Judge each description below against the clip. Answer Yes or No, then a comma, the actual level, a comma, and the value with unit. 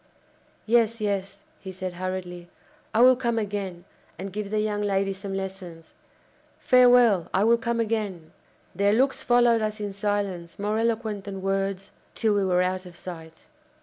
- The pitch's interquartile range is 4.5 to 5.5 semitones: No, average, 2.9 semitones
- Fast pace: No, average, 160 wpm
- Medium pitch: No, high, 200 Hz